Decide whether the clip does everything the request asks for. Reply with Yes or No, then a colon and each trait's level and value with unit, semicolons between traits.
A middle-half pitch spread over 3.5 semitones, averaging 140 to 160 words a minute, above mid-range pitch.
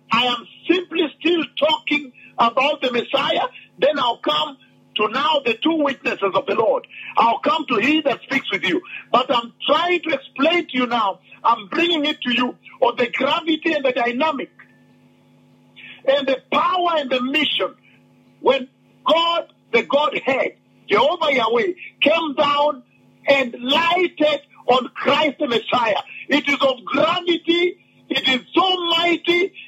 Yes: average, 4.1 semitones; average, 150 wpm; very high, 295 Hz